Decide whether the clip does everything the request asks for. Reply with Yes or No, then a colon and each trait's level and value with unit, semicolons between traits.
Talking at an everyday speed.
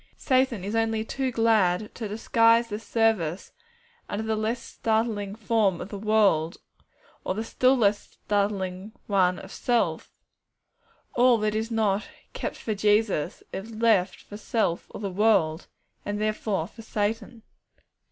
Yes: average, 145 wpm